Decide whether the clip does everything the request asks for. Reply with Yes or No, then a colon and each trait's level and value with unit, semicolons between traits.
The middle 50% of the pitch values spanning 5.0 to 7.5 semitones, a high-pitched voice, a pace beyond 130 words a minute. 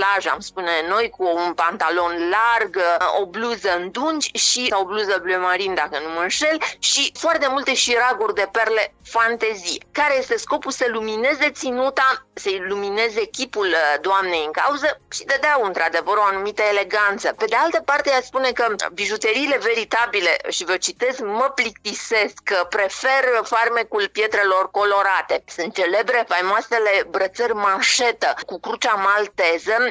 Yes: wide, 5.4 semitones; high, 220 Hz; average, 145 wpm